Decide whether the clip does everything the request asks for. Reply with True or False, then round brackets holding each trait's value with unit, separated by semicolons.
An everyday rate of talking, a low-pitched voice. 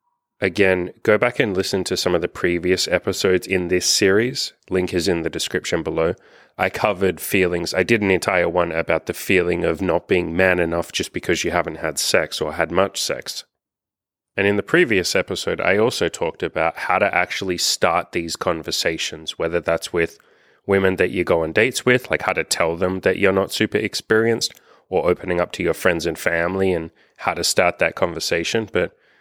True (195 wpm; 95 Hz)